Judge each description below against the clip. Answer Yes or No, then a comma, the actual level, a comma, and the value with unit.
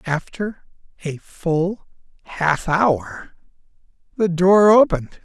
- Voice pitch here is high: No, medium, 175 Hz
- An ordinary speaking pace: No, slow, 90 wpm